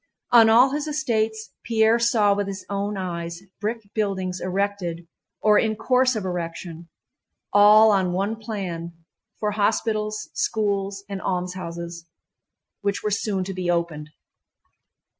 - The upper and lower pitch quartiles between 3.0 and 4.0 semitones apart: Yes, average, 3.3 semitones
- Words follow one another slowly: Yes, slow, 130 wpm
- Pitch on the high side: Yes, high, 200 Hz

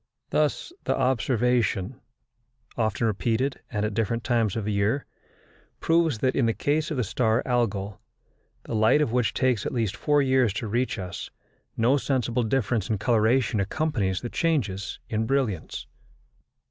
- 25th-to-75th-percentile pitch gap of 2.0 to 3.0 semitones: No, average, 3.7 semitones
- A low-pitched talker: Yes, low, 115 Hz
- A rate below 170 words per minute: Yes, average, 150 wpm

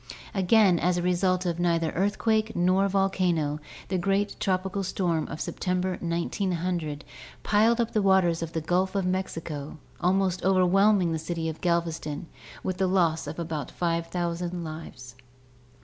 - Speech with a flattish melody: Yes, narrow, 2.3 semitones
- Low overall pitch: No, medium, 180 Hz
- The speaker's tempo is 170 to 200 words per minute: No, average, 150 wpm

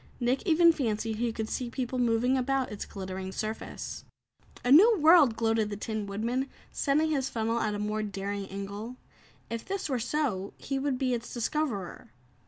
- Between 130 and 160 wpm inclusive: No, average, 175 wpm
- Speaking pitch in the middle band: No, high, 235 Hz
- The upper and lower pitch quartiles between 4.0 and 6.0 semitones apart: Yes, average, 4.3 semitones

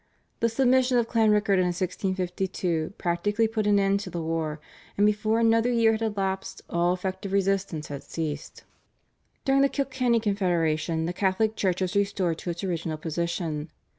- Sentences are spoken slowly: No, average, 160 wpm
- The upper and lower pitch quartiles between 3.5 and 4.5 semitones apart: Yes, average, 4.2 semitones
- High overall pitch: Yes, high, 195 Hz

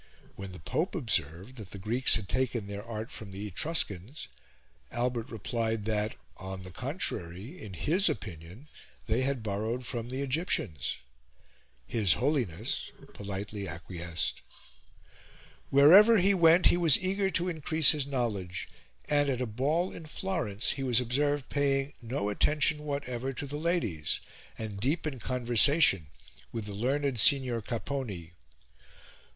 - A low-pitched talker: Yes, low, 120 Hz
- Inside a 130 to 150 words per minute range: Yes, average, 140 wpm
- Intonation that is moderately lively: No, wide, 6.1 semitones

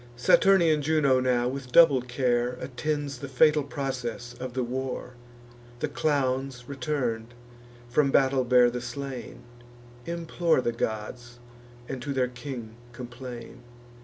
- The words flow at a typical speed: No, slow, 125 wpm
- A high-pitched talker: No, low, 130 Hz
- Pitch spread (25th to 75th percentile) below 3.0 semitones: Yes, narrow, 2.4 semitones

